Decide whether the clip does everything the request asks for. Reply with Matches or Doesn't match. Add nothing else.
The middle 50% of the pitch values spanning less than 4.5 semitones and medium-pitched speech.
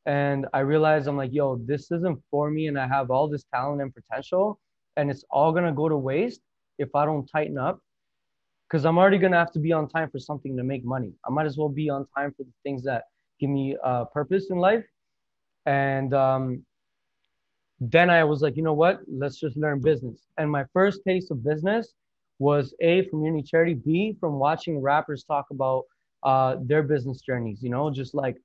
Matches